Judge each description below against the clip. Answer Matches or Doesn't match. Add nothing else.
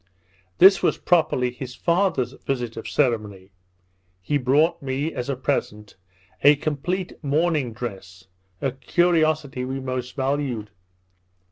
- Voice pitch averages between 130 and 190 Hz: Matches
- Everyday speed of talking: Doesn't match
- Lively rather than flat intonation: Doesn't match